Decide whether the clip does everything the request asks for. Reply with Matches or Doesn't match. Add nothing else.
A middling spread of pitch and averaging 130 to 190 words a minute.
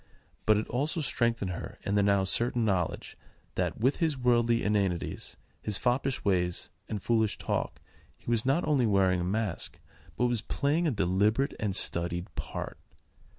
Matches